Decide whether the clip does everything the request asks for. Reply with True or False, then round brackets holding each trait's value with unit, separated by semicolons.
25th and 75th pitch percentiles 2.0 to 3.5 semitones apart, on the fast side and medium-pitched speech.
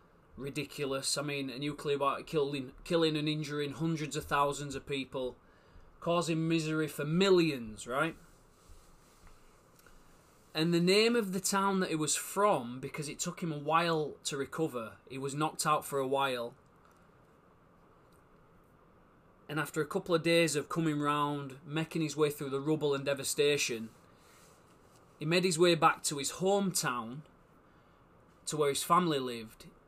False (3.0 semitones; 150 wpm; 150 Hz)